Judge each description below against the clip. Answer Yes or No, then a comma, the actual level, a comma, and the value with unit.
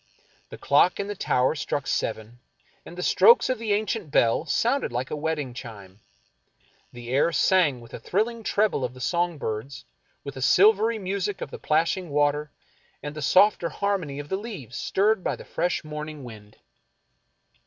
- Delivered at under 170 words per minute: No, average, 175 wpm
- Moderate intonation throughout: No, wide, 7.3 semitones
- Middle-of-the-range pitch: Yes, medium, 155 Hz